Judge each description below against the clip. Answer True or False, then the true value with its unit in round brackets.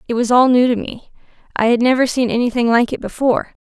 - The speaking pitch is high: True (245 Hz)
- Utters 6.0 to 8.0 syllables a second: True (6.5 syllables/s)